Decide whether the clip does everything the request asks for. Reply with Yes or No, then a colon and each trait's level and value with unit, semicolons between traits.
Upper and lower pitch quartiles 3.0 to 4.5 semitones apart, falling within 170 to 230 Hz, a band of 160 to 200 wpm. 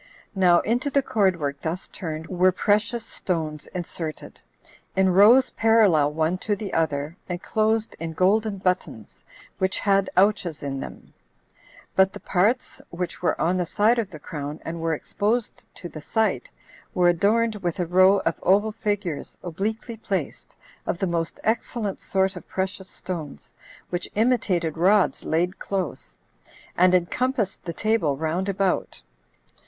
No: average, 4.0 semitones; medium, 185 Hz; average, 145 wpm